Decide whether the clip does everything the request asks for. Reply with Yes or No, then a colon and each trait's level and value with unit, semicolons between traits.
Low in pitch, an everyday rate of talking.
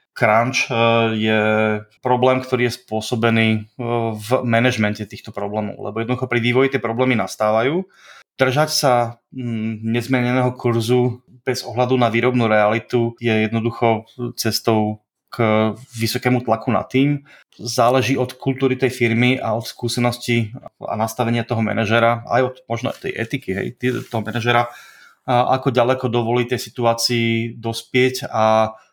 Yes: low, 120 Hz; average, 130 wpm